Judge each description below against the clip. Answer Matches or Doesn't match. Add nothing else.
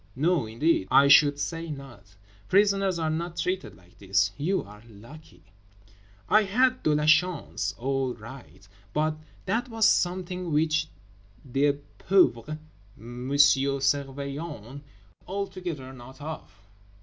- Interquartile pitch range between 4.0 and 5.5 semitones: Matches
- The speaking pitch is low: Doesn't match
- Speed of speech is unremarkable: Doesn't match